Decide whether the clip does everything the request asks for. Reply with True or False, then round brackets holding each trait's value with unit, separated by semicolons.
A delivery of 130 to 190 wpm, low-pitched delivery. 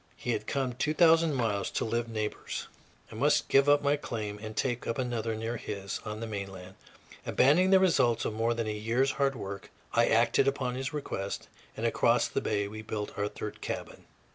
False (200 wpm; 115 Hz)